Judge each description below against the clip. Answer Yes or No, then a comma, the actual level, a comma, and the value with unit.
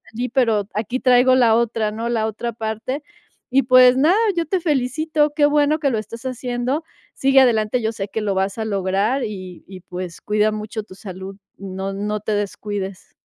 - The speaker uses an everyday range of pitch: Yes, average, 4.0 semitones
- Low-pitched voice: No, high, 220 Hz